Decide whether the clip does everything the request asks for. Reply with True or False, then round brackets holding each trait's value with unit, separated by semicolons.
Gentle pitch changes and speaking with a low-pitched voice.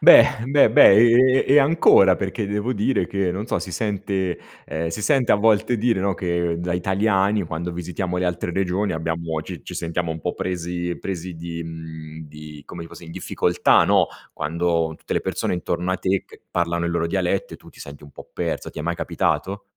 False (3.1 semitones; 90 Hz)